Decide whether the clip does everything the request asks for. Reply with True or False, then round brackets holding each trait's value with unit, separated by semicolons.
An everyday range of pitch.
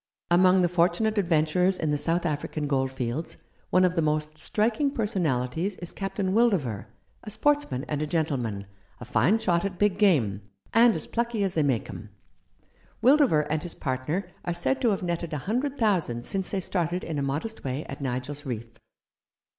False (5.8 semitones)